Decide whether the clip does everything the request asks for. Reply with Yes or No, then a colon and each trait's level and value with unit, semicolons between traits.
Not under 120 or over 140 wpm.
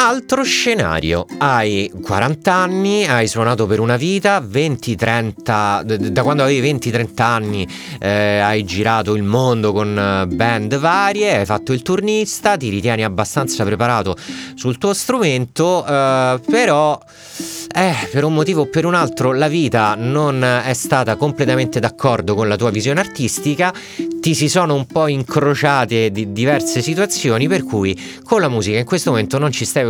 No: average, 155 wpm